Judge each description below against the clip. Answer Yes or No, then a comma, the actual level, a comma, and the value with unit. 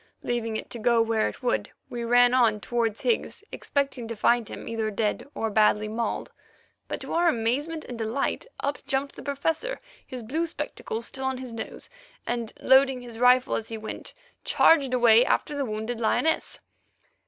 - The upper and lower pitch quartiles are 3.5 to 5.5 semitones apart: No, average, 3.1 semitones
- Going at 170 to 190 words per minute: Yes, average, 175 wpm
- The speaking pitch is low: No, high, 240 Hz